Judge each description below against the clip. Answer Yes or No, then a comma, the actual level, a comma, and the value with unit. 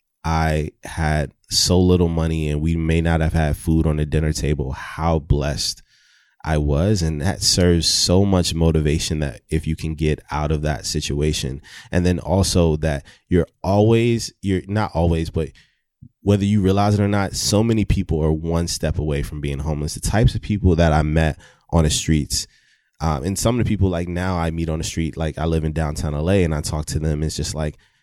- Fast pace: Yes, fast, 210 wpm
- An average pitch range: Yes, average, 3.1 semitones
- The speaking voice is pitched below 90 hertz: Yes, very low, 80 Hz